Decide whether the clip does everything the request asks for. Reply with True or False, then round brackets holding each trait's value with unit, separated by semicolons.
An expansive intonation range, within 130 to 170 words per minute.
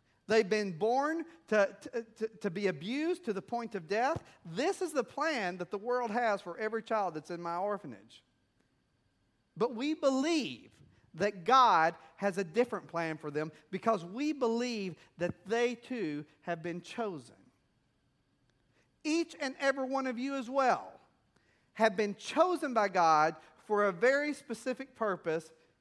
True (6.8 semitones; 155 wpm)